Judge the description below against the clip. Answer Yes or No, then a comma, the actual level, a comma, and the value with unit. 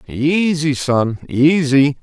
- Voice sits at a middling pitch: Yes, medium, 145 Hz